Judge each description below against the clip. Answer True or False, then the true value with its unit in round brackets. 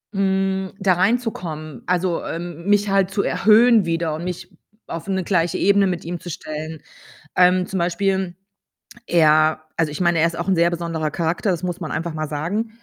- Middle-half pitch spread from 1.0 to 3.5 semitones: True (2.7 semitones)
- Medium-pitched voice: True (175 Hz)